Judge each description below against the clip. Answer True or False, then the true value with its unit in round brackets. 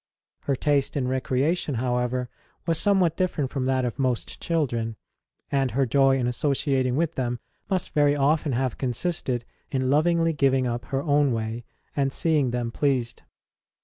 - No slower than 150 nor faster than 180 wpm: True (155 wpm)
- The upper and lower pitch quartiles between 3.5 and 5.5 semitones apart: False (3.0 semitones)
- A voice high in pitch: False (135 Hz)